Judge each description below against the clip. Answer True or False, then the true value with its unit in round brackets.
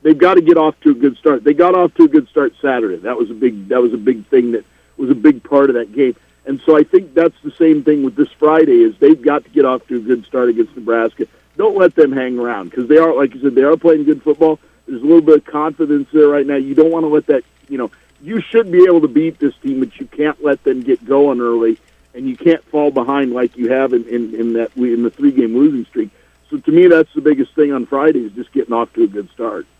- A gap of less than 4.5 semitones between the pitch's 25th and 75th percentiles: False (5.1 semitones)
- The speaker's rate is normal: False (280 wpm)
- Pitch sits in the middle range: True (150 Hz)